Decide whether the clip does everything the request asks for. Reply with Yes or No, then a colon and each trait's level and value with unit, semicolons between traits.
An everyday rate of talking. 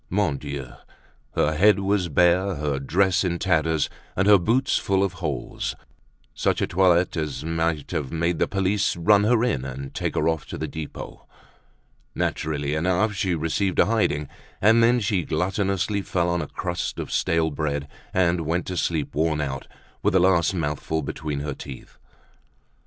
Yes: average, 170 wpm